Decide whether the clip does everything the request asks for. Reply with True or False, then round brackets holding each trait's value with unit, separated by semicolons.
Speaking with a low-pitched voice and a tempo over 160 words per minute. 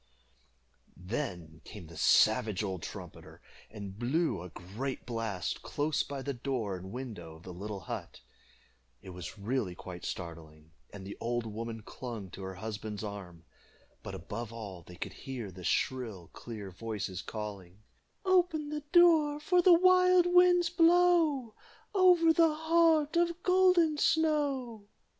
False (115 Hz; 145 wpm)